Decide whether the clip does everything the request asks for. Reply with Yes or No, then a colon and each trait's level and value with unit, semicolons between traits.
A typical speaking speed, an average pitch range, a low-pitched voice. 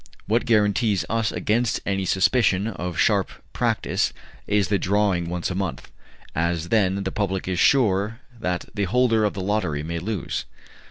Yes: average, 160 wpm; average, 3.2 semitones; low, 100 Hz